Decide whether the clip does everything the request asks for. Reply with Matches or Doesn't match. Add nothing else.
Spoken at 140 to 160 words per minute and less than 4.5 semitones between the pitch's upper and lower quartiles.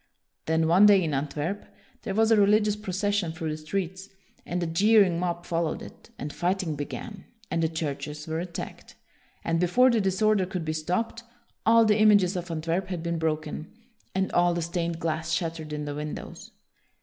Doesn't match